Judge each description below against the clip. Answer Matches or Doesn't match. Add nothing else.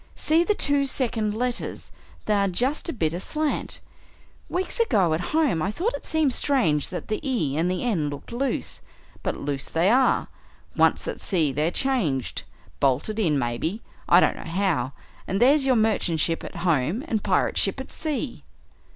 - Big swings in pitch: Matches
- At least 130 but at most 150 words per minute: Doesn't match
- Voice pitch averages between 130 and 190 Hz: Doesn't match